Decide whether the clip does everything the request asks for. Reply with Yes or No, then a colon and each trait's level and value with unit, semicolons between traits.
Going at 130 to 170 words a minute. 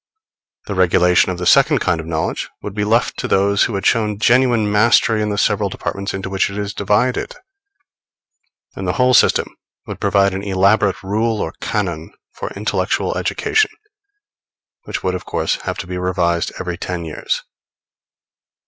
Yes: average, 165 wpm